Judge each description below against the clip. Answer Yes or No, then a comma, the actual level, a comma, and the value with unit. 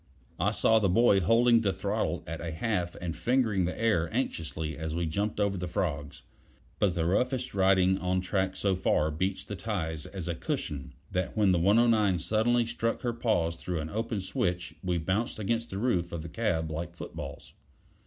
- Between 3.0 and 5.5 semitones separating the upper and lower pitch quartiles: Yes, average, 4.4 semitones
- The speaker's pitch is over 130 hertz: No, very low, 95 Hz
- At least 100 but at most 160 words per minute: No, average, 190 wpm